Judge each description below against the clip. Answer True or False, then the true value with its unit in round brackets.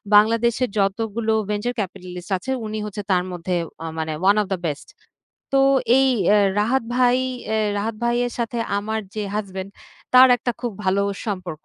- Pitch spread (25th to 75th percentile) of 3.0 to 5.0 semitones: True (3.9 semitones)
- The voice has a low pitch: False (210 Hz)